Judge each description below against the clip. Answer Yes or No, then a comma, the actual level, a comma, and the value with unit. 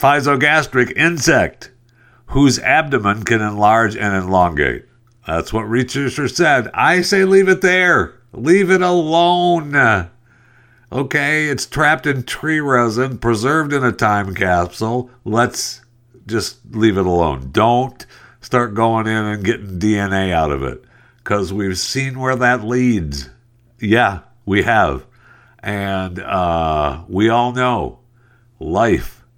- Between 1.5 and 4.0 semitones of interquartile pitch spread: No, average, 4.5 semitones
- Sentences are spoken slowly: Yes, slow, 125 wpm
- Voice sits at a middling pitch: No, low, 120 Hz